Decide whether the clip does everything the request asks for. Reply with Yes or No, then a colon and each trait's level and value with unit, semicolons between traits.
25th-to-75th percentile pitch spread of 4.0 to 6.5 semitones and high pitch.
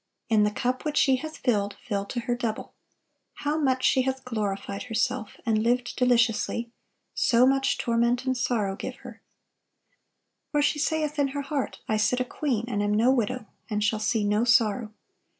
No: average, 3.4 semitones; high, 240 Hz